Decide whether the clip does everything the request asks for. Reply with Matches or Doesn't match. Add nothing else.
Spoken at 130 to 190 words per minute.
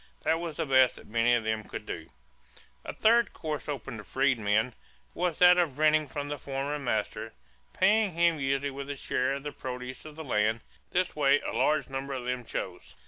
Doesn't match